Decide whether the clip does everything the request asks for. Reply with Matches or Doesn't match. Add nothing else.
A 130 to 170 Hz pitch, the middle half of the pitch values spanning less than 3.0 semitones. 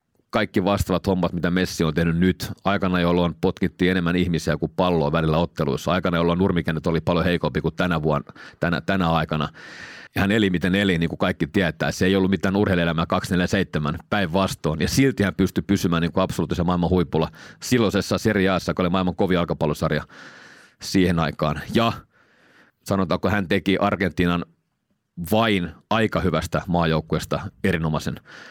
Doesn't match